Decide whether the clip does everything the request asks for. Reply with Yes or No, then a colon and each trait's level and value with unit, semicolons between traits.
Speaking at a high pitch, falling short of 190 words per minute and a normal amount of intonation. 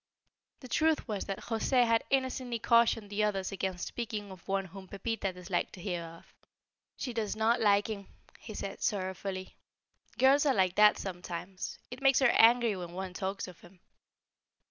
Yes: high, 205 Hz; average, 170 wpm; average, 3.7 semitones